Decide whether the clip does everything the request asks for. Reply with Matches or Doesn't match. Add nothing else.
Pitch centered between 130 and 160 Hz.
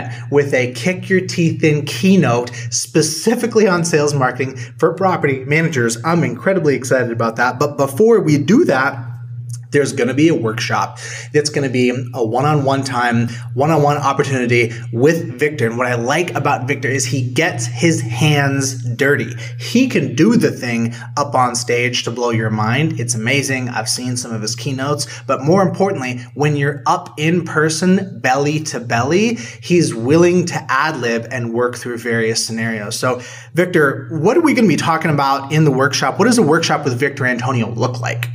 Matches